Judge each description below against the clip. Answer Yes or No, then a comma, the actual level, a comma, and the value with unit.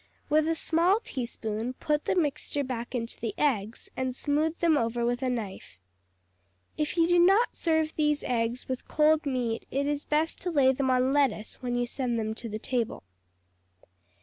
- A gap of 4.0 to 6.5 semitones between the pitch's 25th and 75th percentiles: Yes, average, 4.3 semitones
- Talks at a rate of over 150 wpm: Yes, average, 180 wpm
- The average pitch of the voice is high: Yes, very high, 265 Hz